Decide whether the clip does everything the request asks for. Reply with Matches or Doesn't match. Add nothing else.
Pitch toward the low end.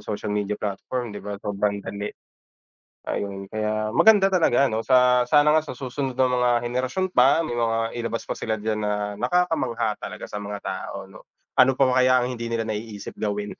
Matches